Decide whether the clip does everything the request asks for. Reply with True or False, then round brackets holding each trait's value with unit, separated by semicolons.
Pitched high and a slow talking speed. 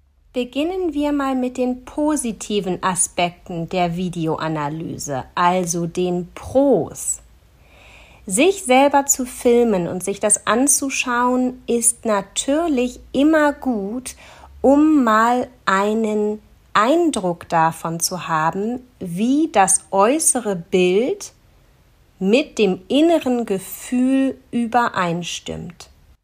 True (215 Hz; 90 wpm)